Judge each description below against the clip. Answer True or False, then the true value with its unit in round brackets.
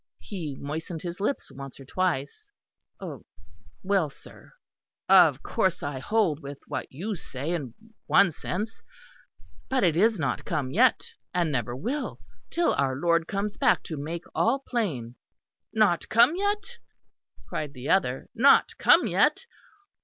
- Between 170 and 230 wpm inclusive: False (140 wpm)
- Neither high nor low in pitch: True (170 Hz)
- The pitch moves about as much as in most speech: False (7.6 semitones)